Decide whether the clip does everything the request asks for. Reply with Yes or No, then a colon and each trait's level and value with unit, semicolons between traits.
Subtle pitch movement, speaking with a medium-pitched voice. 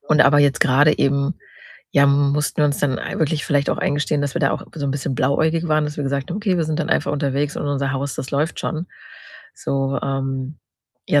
Yes: narrow, 1.7 semitones; medium, 145 Hz